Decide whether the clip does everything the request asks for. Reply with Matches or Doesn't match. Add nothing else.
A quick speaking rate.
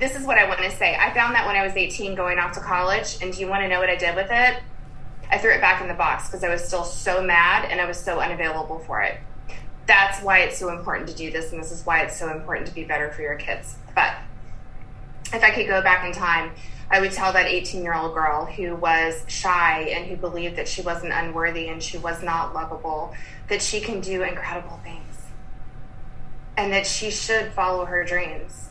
Matches